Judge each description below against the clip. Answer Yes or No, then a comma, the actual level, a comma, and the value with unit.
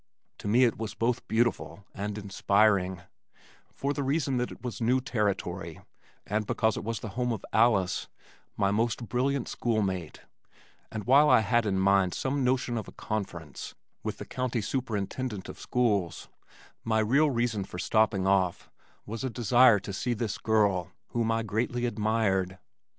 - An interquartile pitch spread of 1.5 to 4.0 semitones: Yes, average, 3.7 semitones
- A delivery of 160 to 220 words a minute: Yes, average, 165 wpm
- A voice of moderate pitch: No, low, 110 Hz